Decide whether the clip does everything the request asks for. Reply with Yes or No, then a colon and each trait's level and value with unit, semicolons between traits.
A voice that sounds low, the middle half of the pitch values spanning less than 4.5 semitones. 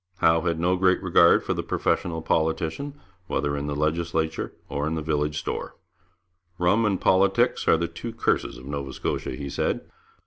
Yes: very low, 80 Hz; average, 3.1 semitones